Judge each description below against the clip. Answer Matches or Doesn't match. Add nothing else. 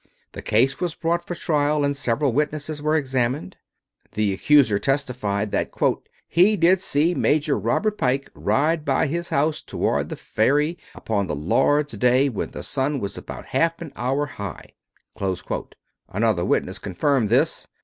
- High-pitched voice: Doesn't match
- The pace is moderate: Matches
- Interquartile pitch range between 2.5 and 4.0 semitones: Doesn't match